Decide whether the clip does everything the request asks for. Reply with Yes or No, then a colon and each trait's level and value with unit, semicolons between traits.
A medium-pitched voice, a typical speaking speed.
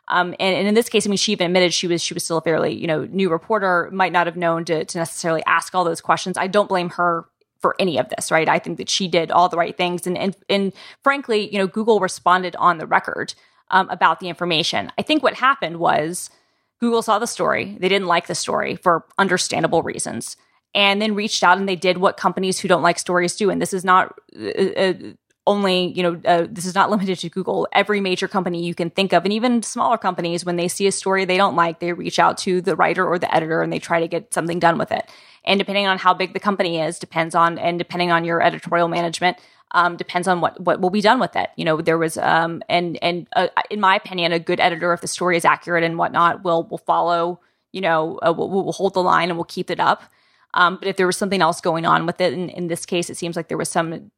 No: medium, 180 Hz; fast, 260 wpm